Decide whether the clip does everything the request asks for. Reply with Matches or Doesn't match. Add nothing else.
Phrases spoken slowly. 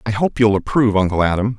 Doesn't match